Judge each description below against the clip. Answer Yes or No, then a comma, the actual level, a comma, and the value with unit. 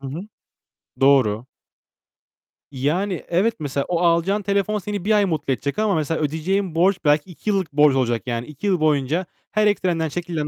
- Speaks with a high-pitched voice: No, medium, 165 Hz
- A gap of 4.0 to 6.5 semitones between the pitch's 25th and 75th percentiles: Yes, wide, 5.5 semitones